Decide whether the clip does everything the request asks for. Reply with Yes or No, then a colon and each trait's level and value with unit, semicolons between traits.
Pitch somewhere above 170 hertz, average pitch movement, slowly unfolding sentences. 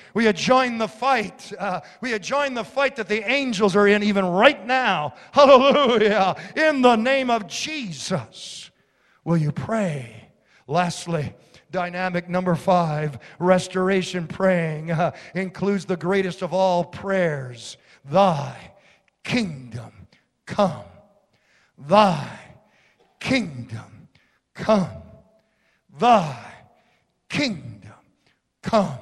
Yes: medium, 185 Hz; average, 4.7 semitones; slow, 100 wpm